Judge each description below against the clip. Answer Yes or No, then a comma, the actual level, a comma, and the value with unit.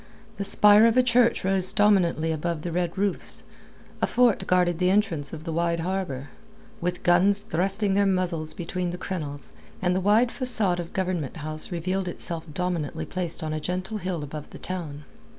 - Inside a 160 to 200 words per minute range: Yes, average, 180 wpm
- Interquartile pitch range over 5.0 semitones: No, average, 2.9 semitones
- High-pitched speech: No, medium, 180 Hz